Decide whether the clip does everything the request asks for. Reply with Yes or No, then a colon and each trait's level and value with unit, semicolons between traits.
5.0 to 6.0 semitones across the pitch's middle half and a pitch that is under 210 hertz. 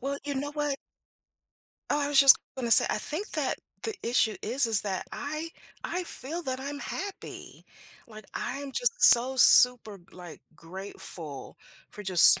No: average, 5.3 semitones; very high, 265 Hz